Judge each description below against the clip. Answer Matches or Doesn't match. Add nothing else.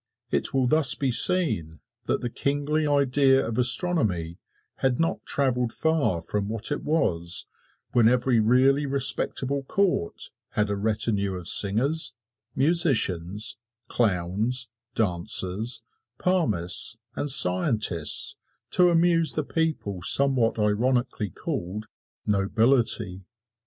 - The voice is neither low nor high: Doesn't match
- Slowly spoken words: Matches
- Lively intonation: Matches